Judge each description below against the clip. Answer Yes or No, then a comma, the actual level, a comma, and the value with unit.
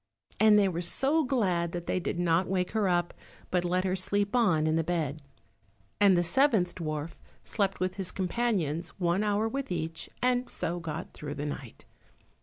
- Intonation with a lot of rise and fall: No, average, 3.6 semitones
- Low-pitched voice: No, medium, 180 Hz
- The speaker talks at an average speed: Yes, average, 185 wpm